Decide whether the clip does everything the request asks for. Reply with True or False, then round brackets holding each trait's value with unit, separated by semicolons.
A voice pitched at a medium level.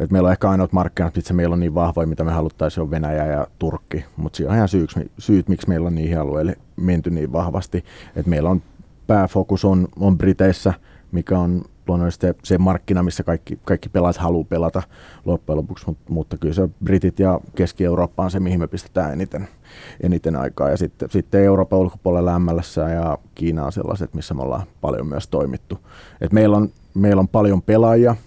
False (90 Hz)